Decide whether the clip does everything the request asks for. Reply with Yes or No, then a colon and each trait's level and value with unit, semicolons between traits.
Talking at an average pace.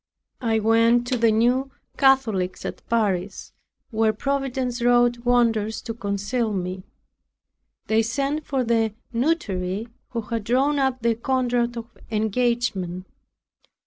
No: slow, 120 wpm